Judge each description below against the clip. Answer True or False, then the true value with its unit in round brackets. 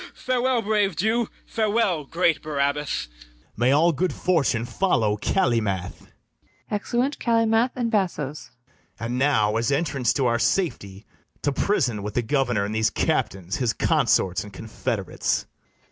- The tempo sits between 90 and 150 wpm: True (135 wpm)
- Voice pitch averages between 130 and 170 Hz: True (140 Hz)